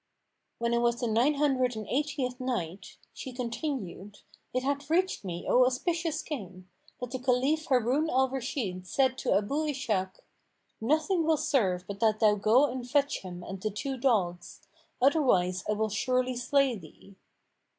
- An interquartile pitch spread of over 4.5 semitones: Yes, average, 5.2 semitones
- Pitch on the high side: Yes, very high, 250 Hz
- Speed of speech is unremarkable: Yes, average, 160 wpm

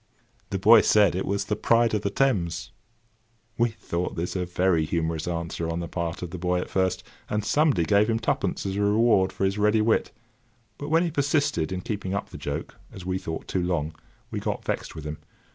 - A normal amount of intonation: Yes, average, 3.8 semitones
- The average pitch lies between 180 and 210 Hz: No, very low, 95 Hz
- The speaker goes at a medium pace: No, fast, 215 wpm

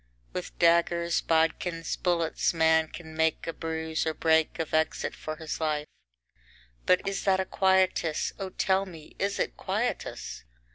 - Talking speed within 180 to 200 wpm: No, average, 150 wpm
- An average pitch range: No, narrow, 2.3 semitones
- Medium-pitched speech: Yes, medium, 165 Hz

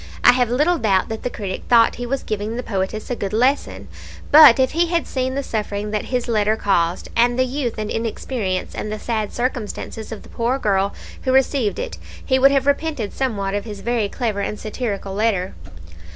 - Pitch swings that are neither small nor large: Yes, average, 3.9 semitones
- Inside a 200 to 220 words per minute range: Yes, fast, 205 wpm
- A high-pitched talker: Yes, high, 230 Hz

